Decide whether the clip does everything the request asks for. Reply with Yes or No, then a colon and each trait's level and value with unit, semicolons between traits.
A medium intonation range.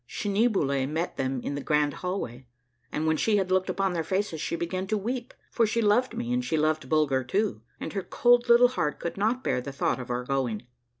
No: wide, 7.5 semitones